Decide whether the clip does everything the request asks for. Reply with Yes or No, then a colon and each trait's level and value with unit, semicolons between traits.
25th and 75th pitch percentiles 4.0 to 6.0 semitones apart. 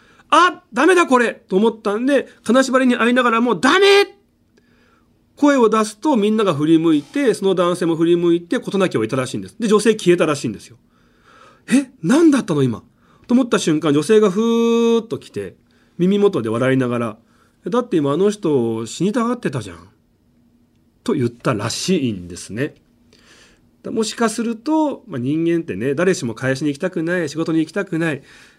No: wide, 8.5 semitones